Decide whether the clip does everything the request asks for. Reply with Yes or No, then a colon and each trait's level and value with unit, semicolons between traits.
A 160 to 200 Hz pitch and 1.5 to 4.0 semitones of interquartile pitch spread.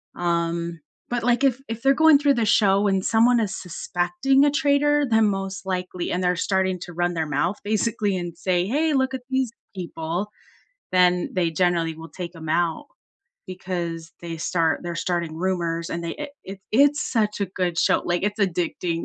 No: medium, 185 Hz; average, 4.8 semitones